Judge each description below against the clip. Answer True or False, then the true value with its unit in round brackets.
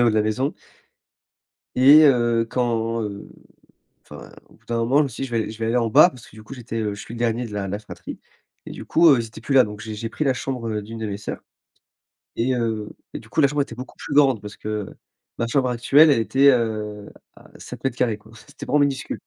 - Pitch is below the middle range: True (115 Hz)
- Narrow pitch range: False (3.3 semitones)